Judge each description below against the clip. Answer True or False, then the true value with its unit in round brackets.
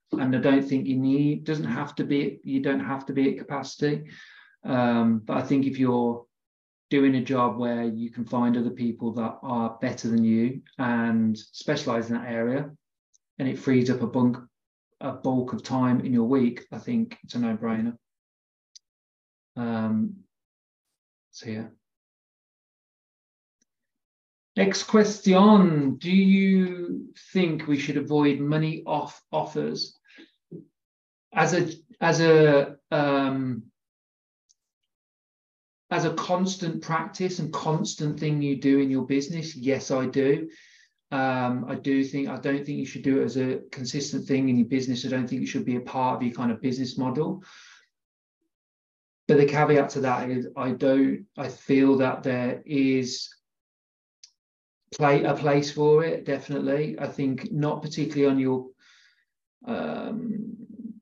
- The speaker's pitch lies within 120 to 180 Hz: True (135 Hz)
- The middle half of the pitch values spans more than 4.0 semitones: False (3.7 semitones)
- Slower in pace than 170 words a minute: True (150 wpm)